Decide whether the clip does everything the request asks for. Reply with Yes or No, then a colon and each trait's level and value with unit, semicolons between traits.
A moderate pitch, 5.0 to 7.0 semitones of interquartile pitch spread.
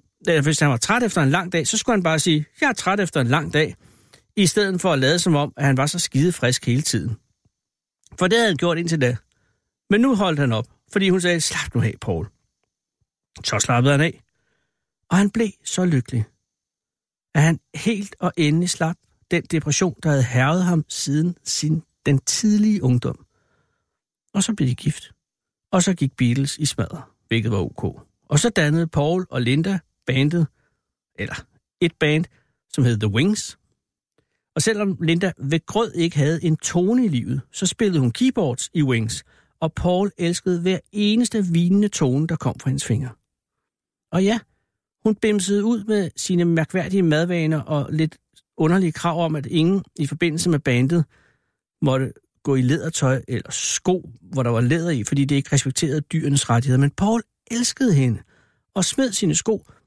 Yes: medium, 160 Hz; wide, 5.6 semitones